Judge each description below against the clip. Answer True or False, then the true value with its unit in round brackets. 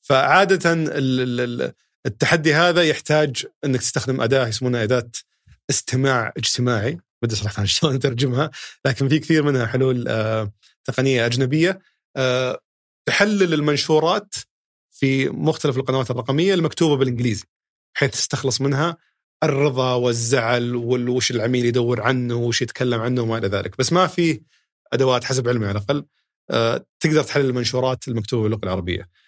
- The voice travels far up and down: False (3.8 semitones)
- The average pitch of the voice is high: False (130 Hz)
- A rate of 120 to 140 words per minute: True (125 wpm)